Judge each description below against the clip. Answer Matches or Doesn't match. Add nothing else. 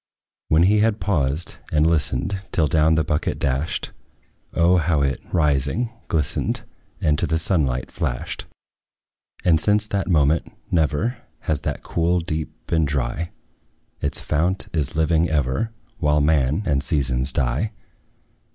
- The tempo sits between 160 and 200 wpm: Doesn't match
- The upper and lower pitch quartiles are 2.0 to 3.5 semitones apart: Matches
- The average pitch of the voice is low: Matches